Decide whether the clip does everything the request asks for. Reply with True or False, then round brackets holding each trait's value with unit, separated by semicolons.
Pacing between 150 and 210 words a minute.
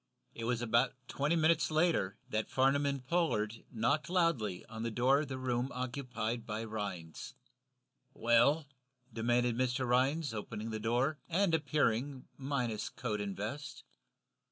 False (140 wpm)